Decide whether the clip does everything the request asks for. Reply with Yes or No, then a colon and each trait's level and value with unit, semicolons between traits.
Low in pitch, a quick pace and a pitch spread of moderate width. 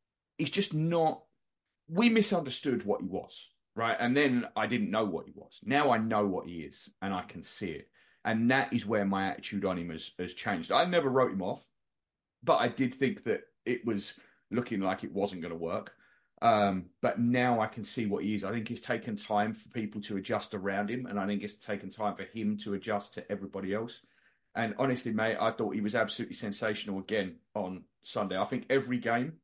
Yes: low, 110 Hz; fast, 220 wpm; average, 3.6 semitones